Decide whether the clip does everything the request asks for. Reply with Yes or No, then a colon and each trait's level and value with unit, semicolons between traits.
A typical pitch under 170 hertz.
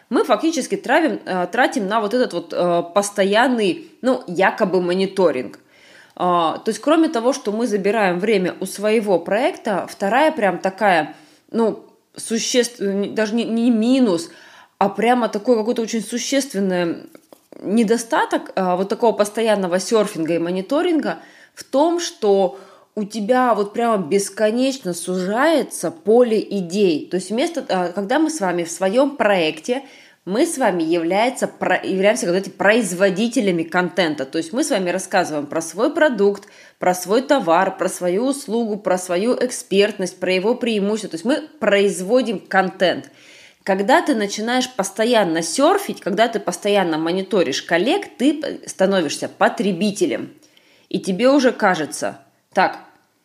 No: high, 210 Hz